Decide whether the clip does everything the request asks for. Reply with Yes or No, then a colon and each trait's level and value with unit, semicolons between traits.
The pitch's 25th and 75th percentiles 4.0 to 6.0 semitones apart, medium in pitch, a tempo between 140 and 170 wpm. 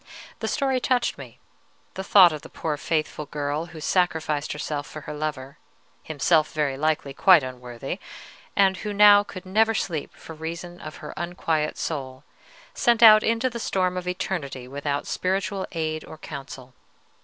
Yes: average, 4.4 semitones; medium, 160 Hz; average, 160 wpm